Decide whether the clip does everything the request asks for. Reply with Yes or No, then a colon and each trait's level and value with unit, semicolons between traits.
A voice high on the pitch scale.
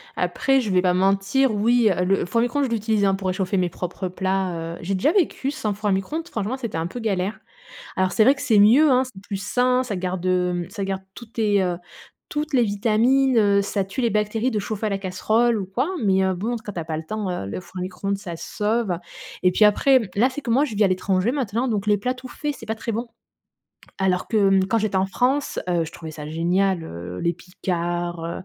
Yes: high, 200 Hz